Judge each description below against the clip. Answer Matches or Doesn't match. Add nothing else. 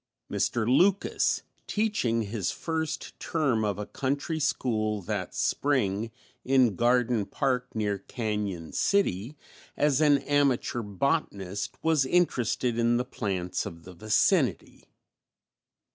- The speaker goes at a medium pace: Doesn't match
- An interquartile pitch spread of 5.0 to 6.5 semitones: Matches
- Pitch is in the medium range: Doesn't match